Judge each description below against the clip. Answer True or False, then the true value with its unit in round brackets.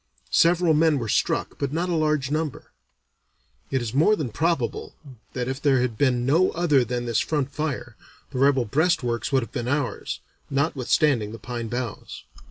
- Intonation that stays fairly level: False (4.1 semitones)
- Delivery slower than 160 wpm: False (175 wpm)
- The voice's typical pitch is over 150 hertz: False (135 Hz)